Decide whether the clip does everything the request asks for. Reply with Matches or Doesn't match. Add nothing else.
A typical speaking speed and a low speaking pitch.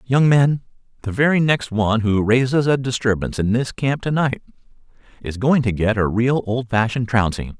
Matches